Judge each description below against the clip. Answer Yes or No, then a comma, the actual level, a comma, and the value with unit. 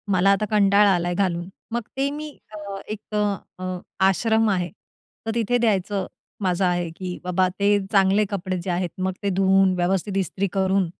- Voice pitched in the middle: No, high, 195 Hz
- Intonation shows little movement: Yes, narrow, 2.1 semitones